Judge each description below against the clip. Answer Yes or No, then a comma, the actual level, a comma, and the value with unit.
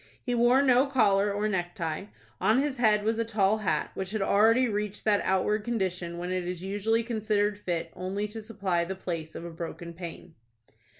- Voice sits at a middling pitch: No, high, 205 Hz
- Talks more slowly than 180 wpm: No, average, 190 wpm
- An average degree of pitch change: Yes, average, 3.6 semitones